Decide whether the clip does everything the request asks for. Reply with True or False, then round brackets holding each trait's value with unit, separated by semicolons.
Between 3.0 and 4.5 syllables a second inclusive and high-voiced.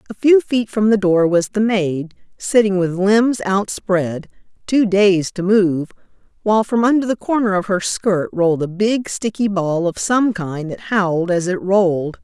True (4.4 syllables/s; 195 Hz)